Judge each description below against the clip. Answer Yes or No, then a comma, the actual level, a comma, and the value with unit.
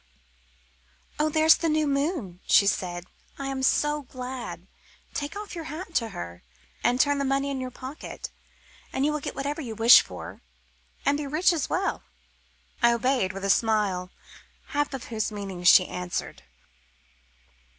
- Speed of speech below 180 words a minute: Yes, average, 160 wpm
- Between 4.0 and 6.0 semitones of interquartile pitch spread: Yes, wide, 5.6 semitones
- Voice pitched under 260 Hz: No, very high, 265 Hz